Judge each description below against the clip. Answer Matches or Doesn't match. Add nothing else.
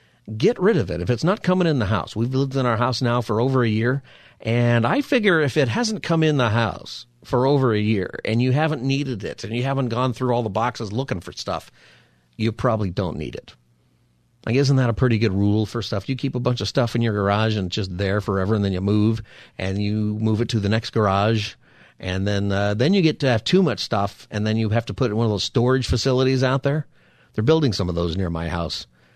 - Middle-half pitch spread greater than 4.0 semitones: Matches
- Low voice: Matches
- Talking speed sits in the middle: Doesn't match